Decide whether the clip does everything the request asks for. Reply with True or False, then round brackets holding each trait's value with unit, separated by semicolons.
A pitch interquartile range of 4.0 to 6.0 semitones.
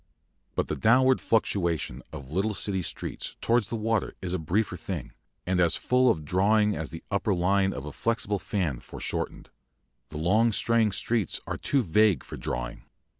True (4.5 semitones)